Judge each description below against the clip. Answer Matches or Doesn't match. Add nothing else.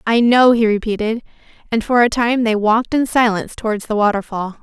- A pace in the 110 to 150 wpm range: Doesn't match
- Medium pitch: Doesn't match